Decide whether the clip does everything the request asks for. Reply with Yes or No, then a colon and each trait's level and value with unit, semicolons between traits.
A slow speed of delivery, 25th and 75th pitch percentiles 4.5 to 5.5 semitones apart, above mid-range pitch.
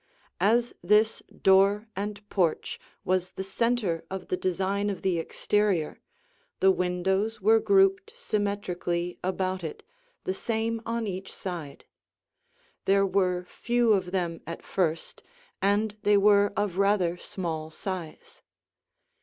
No: slow, 125 wpm; narrow, 2.6 semitones; high, 195 Hz